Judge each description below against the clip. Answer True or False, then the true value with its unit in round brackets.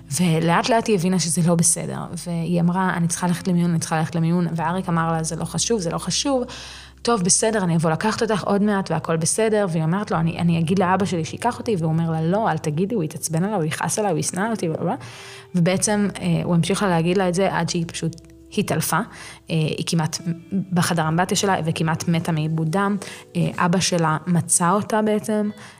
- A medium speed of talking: False (200 wpm)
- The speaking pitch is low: False (175 Hz)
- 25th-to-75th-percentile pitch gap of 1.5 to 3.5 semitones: True (3.0 semitones)